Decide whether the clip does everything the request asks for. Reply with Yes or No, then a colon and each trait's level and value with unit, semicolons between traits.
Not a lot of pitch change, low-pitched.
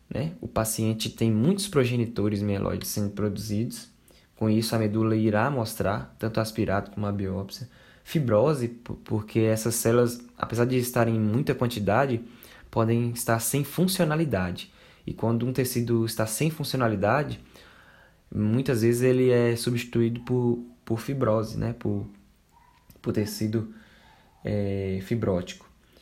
Yes: narrow, 2.3 semitones; low, 115 Hz